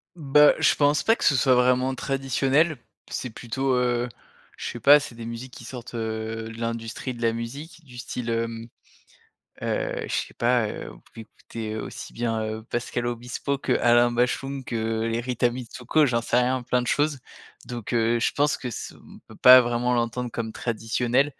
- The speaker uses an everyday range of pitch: No, narrow, 2.2 semitones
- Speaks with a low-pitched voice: Yes, low, 120 Hz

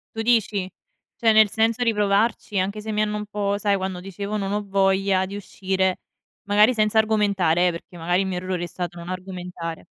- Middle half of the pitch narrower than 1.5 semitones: No, narrow, 2.4 semitones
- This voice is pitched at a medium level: No, high, 200 Hz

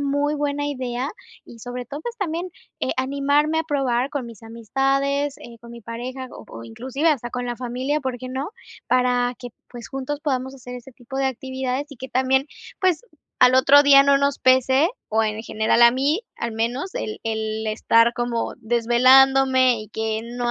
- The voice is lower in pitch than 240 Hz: No, very high, 255 Hz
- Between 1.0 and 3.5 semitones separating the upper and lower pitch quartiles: Yes, average, 2.8 semitones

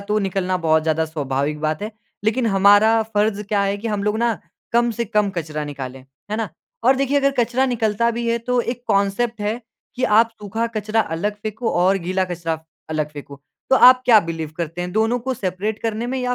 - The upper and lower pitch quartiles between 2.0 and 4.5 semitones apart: No, average, 4.9 semitones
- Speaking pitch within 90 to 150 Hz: No, high, 210 Hz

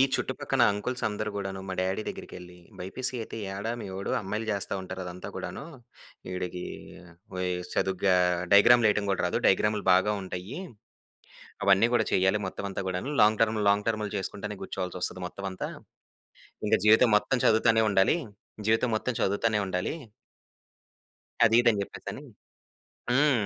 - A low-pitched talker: Yes, low, 100 Hz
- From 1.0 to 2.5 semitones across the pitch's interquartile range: No, average, 2.9 semitones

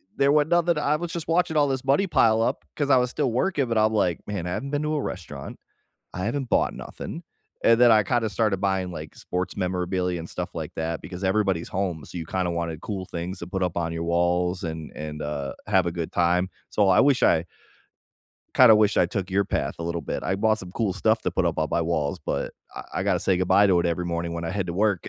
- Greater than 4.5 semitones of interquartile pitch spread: Yes, average, 4.9 semitones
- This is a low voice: Yes, very low, 95 Hz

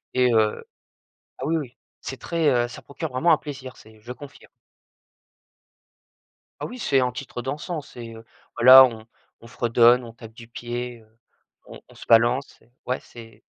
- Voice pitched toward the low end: Yes, low, 125 Hz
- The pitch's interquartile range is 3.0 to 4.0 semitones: No, narrow, 2.6 semitones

